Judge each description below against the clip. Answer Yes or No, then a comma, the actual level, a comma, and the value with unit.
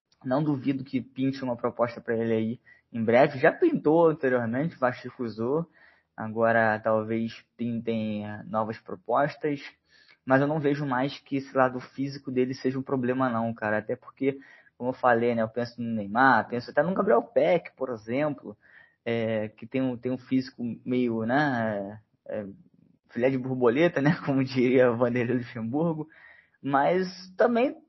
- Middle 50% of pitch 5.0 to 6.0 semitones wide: No, average, 3.1 semitones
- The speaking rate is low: No, average, 155 wpm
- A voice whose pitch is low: Yes, low, 125 Hz